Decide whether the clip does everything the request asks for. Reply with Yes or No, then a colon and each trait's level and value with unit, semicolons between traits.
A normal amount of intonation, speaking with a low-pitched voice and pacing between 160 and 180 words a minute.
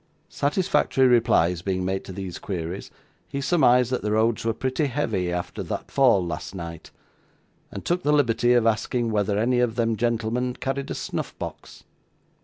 Yes: average, 4.6 semitones; low, 115 Hz; average, 170 wpm